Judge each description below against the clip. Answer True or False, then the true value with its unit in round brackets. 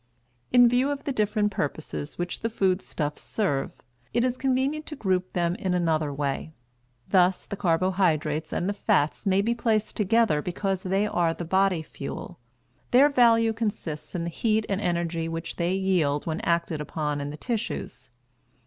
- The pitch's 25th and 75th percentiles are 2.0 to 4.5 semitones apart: False (5.0 semitones)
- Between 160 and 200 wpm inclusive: True (165 wpm)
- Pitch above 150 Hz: True (185 Hz)